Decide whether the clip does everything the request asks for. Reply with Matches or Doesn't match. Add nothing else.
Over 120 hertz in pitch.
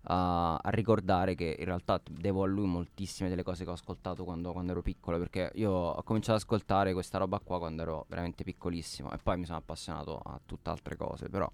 Doesn't match